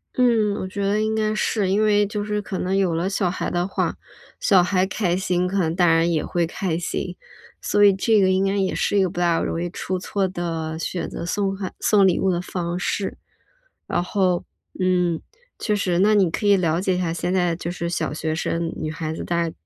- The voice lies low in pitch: No, medium, 185 Hz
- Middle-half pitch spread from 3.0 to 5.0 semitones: No, narrow, 2.6 semitones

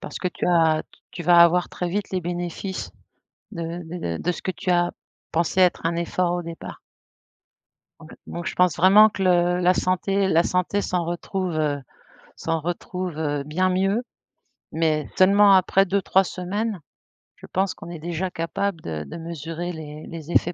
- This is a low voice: No, medium, 175 Hz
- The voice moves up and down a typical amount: No, narrow, 2.1 semitones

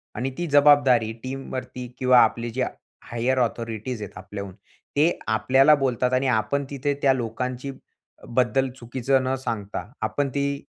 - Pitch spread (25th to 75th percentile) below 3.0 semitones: Yes, narrow, 2.6 semitones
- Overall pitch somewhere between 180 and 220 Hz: No, low, 130 Hz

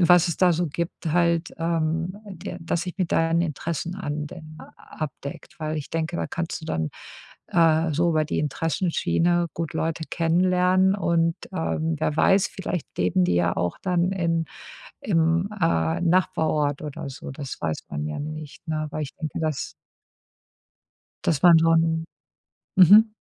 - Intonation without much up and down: Yes, narrow, 2.1 semitones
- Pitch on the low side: No, medium, 165 Hz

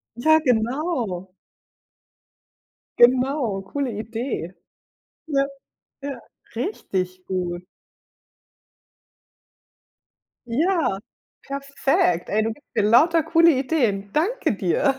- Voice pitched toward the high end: Yes, very high, 250 Hz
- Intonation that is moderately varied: No, wide, 6.9 semitones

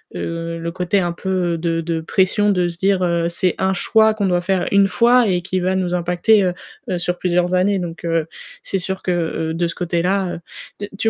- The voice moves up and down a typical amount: No, narrow, 2.0 semitones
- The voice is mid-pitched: Yes, medium, 180 Hz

